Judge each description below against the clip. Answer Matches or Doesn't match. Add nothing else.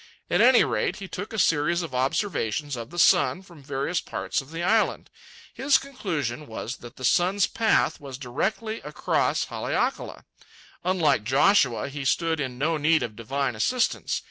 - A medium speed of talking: Matches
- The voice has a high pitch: Doesn't match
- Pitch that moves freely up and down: Matches